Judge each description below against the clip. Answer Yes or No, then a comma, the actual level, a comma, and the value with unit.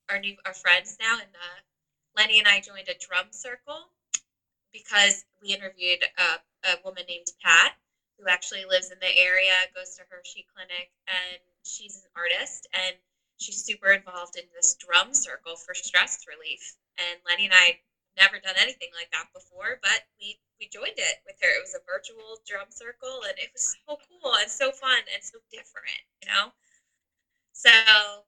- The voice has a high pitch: Yes, high, 195 Hz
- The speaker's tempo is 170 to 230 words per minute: Yes, average, 175 wpm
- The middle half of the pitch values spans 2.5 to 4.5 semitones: No, average, 5.0 semitones